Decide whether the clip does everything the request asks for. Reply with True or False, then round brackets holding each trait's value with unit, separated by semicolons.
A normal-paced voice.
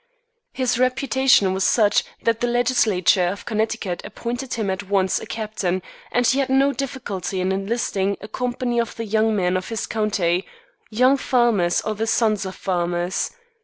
True (165 wpm)